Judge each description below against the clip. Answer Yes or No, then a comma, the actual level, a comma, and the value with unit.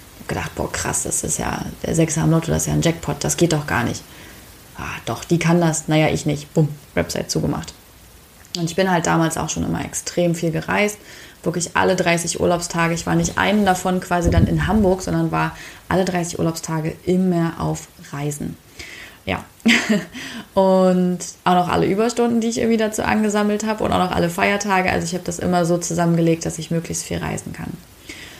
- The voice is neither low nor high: Yes, medium, 170 Hz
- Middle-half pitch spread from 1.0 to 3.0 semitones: Yes, average, 2.7 semitones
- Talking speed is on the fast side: Yes, fast, 195 wpm